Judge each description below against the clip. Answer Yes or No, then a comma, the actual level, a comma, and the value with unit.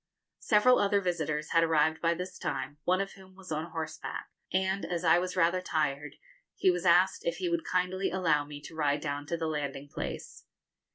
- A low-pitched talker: No, medium, 170 Hz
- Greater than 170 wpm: Yes, average, 195 wpm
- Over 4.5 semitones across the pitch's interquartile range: No, average, 3.6 semitones